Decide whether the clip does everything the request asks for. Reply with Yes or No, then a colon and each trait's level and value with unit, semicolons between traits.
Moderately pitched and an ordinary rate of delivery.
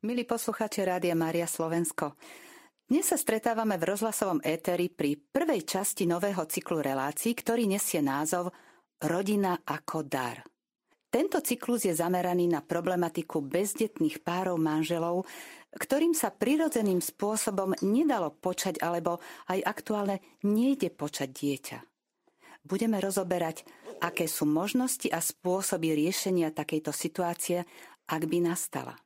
Yes: medium, 180 Hz; average, 120 wpm